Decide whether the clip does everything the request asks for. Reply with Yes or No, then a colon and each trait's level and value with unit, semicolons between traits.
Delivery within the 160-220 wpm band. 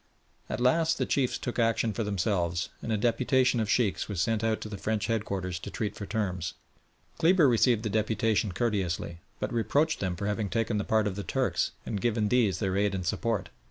Yes: fast, 205 wpm